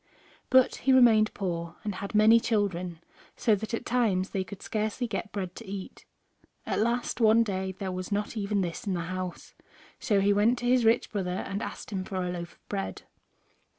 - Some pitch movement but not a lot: Yes, average, 3.3 semitones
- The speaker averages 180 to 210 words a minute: Yes, average, 200 wpm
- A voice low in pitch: No, high, 200 Hz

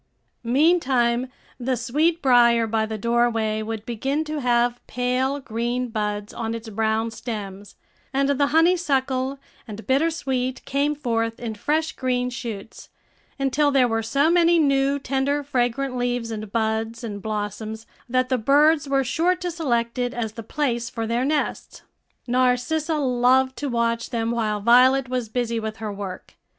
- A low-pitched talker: No, high, 245 Hz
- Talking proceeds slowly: No, average, 155 wpm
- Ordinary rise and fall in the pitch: Yes, average, 3.3 semitones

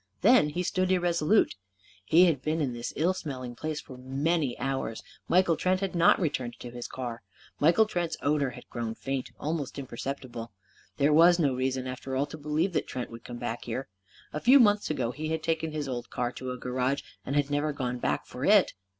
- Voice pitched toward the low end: No, medium, 145 Hz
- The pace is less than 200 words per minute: No, fast, 205 wpm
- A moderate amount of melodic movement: Yes, average, 4.6 semitones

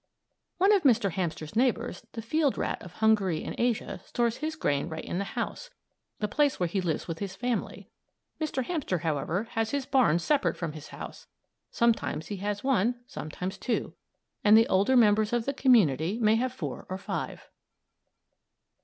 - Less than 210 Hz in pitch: No, high, 215 Hz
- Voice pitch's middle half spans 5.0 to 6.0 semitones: Yes, wide, 5.6 semitones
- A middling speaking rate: Yes, average, 175 wpm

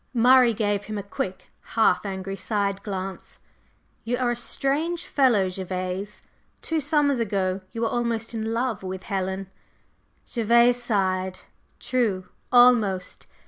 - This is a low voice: No, high, 215 Hz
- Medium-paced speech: No, slow, 130 wpm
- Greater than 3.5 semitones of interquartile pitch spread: Yes, average, 4.1 semitones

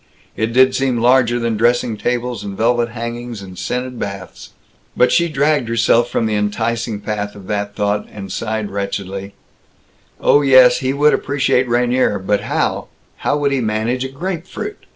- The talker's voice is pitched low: Yes, low, 120 Hz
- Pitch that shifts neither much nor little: Yes, average, 3.7 semitones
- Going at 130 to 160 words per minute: No, average, 170 wpm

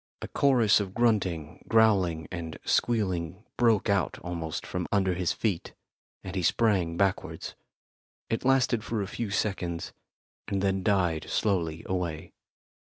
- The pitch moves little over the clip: No, average, 4.0 semitones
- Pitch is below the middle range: Yes, very low, 95 Hz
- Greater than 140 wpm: No, slow, 135 wpm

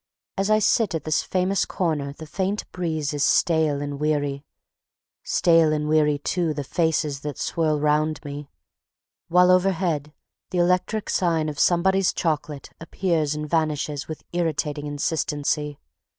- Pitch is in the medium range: Yes, medium, 155 Hz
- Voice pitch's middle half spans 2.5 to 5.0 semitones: Yes, average, 2.9 semitones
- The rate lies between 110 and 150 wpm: Yes, average, 140 wpm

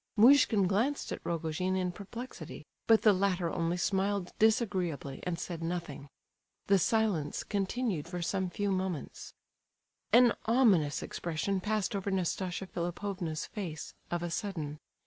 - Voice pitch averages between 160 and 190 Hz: Yes, medium, 185 Hz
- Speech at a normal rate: No, slow, 130 wpm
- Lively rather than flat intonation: No, average, 3.3 semitones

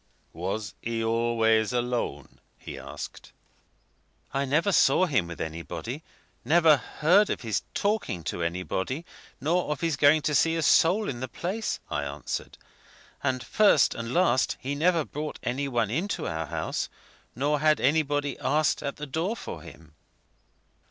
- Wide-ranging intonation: Yes, wide, 5.9 semitones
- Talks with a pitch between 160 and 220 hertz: No, medium, 140 Hz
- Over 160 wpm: No, average, 150 wpm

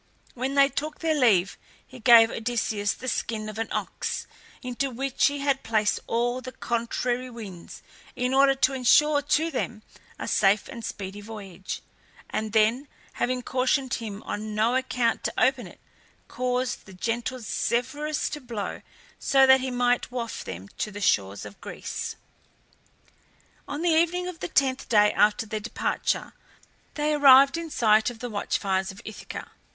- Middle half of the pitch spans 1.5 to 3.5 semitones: No, average, 3.9 semitones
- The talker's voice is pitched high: Yes, high, 245 Hz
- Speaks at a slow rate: No, average, 165 wpm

